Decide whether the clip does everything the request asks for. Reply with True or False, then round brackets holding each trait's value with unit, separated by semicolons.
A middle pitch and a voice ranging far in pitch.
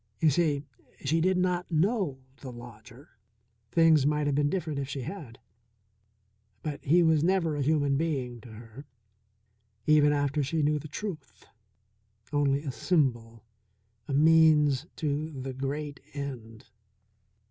False (145 Hz; 3.0 semitones)